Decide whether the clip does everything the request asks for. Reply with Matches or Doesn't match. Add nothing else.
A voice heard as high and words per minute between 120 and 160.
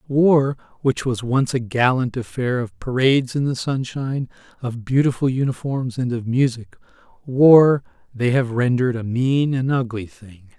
Doesn't match